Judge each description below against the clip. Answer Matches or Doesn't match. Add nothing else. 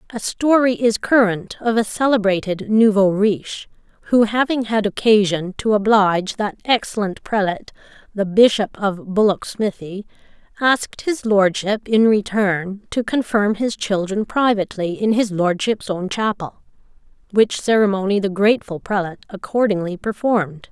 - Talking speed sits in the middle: Doesn't match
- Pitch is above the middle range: Matches